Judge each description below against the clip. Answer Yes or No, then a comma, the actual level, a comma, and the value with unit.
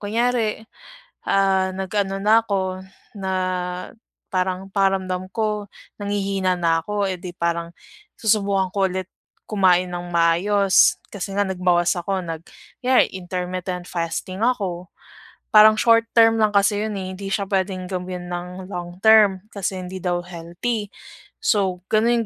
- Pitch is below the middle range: No, high, 190 Hz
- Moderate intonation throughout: No, narrow, 2.2 semitones